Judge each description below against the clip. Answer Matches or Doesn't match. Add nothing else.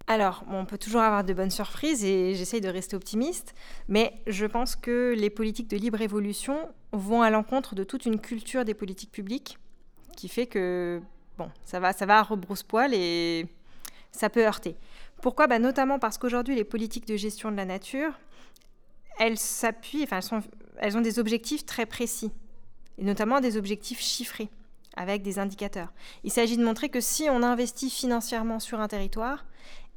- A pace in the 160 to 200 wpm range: Matches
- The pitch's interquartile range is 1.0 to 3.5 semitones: Matches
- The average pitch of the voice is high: Matches